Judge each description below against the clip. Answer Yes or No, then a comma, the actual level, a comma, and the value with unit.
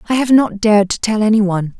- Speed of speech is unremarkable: No, fast, 235 wpm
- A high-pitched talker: Yes, high, 215 Hz